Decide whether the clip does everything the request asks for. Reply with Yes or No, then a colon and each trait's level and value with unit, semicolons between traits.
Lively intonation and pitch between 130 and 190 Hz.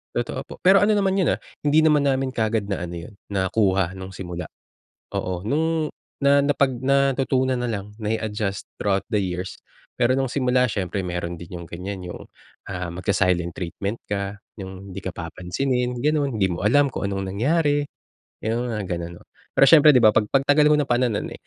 No: wide, 6.5 semitones; low, 110 Hz